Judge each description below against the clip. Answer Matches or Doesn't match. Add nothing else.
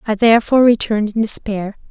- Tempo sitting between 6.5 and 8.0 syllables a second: Matches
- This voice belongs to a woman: Matches